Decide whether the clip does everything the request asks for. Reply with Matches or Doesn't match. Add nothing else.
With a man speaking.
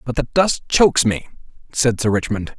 Matches